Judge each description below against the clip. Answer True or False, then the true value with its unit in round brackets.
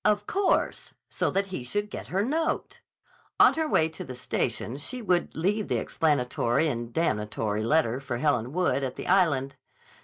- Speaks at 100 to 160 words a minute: False (175 wpm)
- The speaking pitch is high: False (155 Hz)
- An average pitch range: False (7.9 semitones)